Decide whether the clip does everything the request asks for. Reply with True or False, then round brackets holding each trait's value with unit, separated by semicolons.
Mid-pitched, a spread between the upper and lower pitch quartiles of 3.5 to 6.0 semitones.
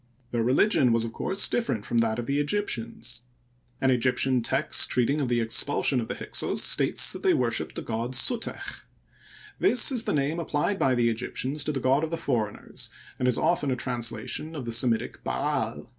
False (125 Hz; 4.0 semitones)